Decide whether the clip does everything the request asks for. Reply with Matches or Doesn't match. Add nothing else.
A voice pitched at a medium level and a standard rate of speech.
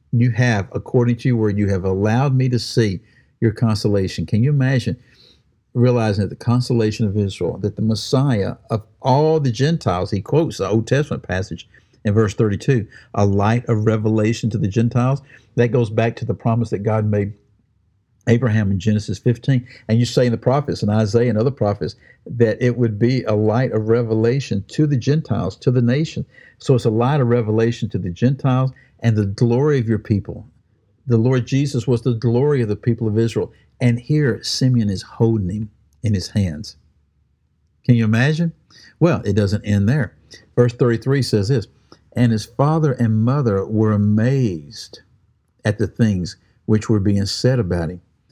Doesn't match